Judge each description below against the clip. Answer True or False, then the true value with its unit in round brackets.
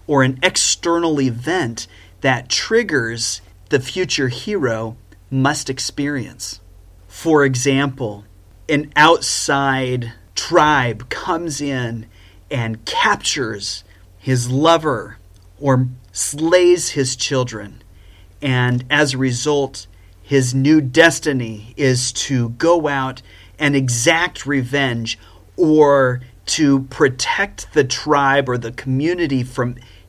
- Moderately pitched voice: False (130 Hz)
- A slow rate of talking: True (100 wpm)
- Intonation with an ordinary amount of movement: True (5.0 semitones)